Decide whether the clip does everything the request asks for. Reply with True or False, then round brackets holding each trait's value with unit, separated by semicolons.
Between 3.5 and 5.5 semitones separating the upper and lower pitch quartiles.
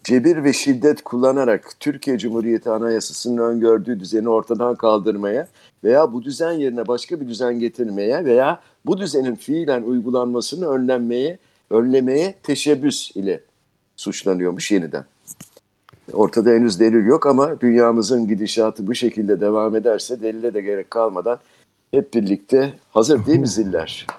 False (2.9 semitones)